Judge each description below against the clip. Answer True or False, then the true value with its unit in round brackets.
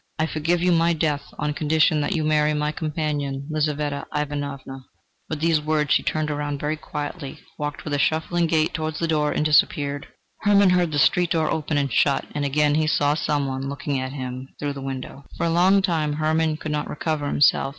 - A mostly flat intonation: True (1.7 semitones)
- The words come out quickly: True (210 wpm)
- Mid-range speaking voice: True (150 Hz)